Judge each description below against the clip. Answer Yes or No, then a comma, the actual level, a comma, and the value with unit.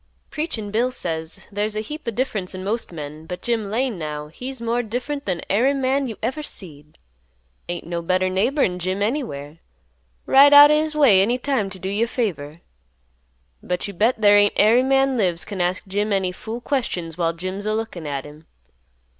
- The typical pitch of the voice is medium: No, high, 205 Hz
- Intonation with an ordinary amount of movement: No, wide, 5.7 semitones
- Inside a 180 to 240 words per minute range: Yes, average, 195 wpm